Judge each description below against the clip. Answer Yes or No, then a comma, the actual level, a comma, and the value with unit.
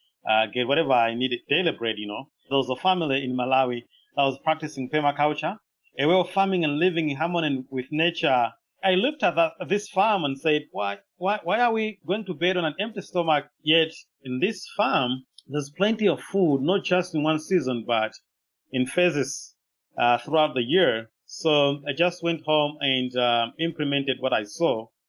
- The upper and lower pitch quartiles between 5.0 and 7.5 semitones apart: Yes, wide, 5.5 semitones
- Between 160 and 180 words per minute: No, average, 190 wpm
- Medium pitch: Yes, medium, 150 Hz